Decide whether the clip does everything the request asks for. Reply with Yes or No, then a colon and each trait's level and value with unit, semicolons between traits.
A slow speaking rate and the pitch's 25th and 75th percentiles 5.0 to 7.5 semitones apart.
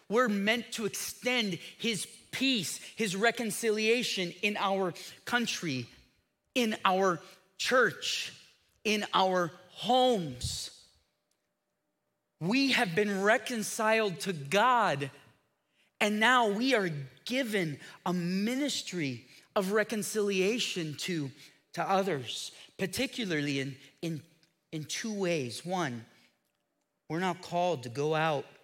Yes: slow, 100 wpm; average, 5.3 semitones